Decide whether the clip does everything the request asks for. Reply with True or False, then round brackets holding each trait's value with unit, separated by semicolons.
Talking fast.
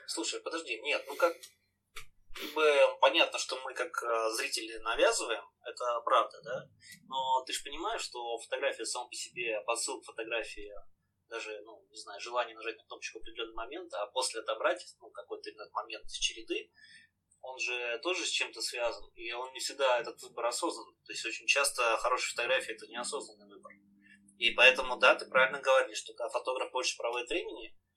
True (170 wpm)